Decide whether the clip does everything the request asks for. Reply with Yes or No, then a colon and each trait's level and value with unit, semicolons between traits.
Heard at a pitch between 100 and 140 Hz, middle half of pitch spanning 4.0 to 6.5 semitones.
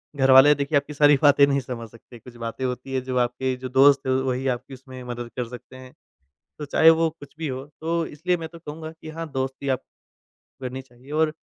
No: low, 135 Hz; average, 2.7 semitones